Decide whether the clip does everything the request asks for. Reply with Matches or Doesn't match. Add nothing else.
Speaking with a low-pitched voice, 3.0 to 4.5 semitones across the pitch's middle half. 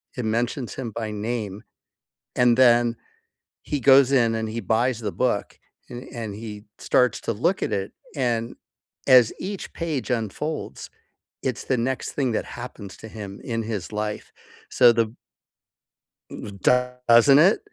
Doesn't match